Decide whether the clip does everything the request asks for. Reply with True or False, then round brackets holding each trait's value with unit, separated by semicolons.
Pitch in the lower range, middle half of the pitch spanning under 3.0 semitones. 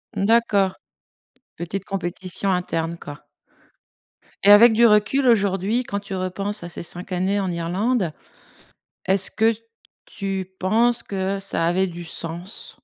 False (195 Hz; 2.6 semitones)